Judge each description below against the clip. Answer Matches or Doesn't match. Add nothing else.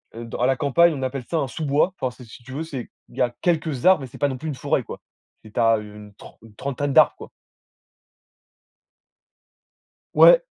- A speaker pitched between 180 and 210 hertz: Doesn't match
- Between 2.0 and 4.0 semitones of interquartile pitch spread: Doesn't match